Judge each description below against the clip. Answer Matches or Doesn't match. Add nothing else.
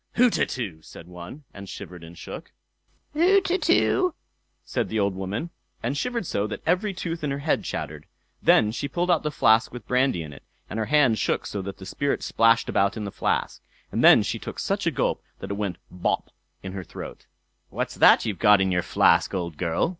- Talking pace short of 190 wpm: Doesn't match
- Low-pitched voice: Matches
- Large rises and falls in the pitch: Matches